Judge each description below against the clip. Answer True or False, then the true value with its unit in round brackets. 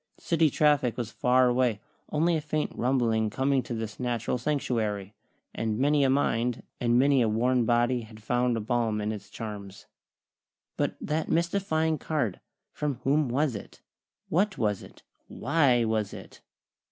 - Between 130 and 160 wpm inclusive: True (155 wpm)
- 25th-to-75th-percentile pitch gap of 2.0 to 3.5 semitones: False (4.6 semitones)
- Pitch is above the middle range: False (125 Hz)